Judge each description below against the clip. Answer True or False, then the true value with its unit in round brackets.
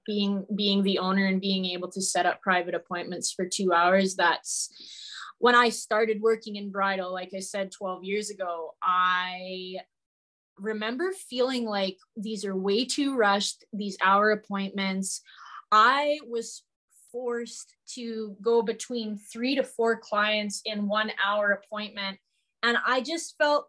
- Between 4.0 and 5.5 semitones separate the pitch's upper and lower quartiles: False (3.2 semitones)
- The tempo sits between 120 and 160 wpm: True (145 wpm)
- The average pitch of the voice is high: True (205 Hz)